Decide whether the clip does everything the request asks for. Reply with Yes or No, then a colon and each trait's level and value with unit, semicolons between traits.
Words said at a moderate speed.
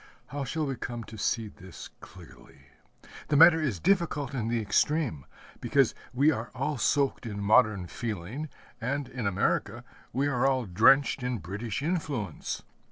Yes: average, 155 wpm